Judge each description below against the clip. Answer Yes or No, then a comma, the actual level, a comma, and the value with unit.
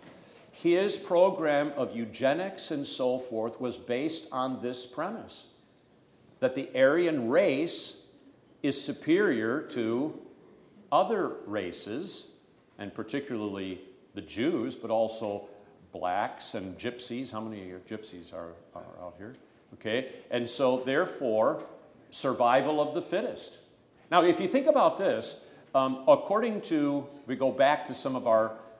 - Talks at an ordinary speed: No, slow, 130 wpm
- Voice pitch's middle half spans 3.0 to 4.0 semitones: No, average, 5.0 semitones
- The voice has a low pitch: Yes, low, 125 Hz